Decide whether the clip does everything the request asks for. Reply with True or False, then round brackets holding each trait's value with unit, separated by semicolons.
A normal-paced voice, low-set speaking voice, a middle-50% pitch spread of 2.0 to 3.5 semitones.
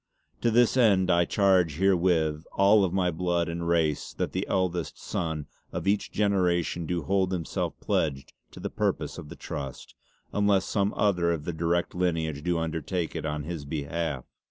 True (175 wpm; 85 Hz; 2.9 semitones)